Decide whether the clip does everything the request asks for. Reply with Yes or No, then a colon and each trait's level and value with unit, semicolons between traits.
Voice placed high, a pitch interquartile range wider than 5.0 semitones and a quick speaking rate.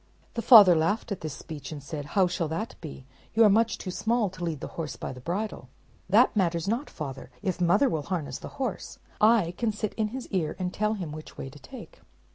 No: medium, 180 Hz; wide, 5.6 semitones; fast, 230 wpm